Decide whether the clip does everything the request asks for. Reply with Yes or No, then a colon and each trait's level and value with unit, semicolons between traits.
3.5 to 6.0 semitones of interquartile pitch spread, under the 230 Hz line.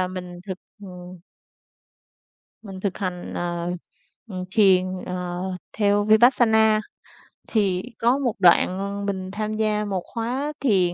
No: average, 3.0 semitones; high, 195 Hz